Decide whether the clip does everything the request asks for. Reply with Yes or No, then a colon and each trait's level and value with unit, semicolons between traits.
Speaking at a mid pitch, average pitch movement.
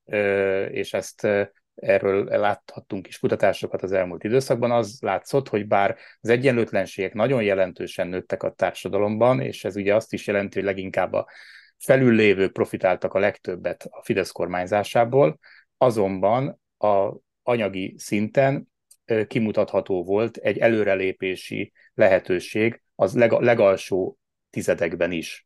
No: low, 105 Hz; average, 3.4 semitones